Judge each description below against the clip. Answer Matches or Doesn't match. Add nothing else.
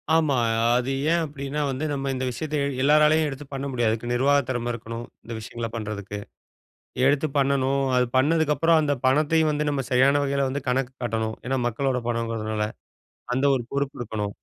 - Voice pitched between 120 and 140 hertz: Matches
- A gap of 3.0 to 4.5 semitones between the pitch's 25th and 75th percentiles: Matches